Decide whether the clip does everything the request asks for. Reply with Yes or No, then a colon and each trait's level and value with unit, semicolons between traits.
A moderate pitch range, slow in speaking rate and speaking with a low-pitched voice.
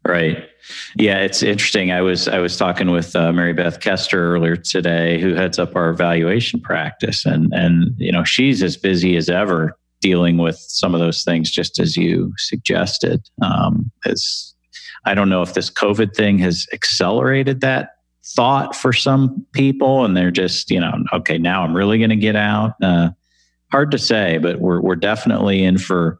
No: average, 3.6 semitones; average, 185 wpm; very low, 90 Hz